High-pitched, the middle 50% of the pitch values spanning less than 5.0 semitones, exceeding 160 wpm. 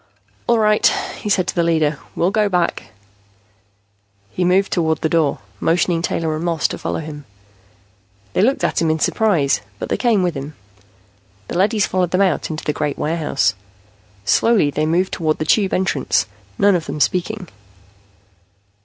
No: medium, 170 Hz; average, 3.8 semitones; average, 170 wpm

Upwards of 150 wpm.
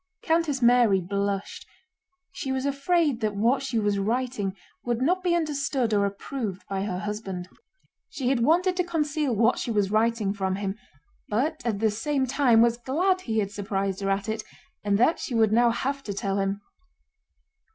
Yes: average, 180 wpm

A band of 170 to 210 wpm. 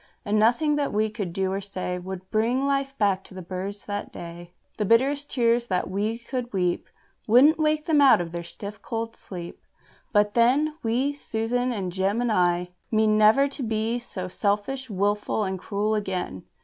Yes: average, 190 wpm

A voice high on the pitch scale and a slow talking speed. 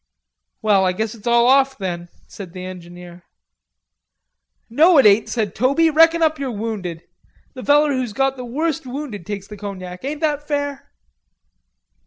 No: high, 235 Hz; average, 160 wpm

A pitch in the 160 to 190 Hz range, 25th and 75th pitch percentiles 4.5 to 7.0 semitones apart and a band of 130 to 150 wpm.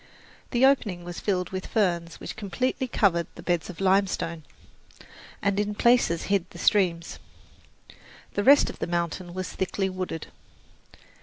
No: medium, 185 Hz; average, 3.0 semitones; average, 145 wpm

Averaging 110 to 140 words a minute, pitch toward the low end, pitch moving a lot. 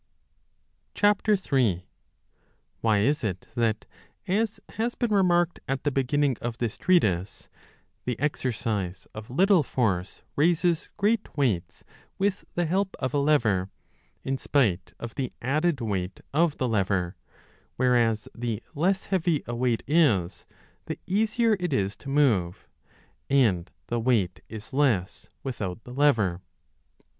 Yes: slow, 135 wpm; low, 130 Hz; wide, 7.8 semitones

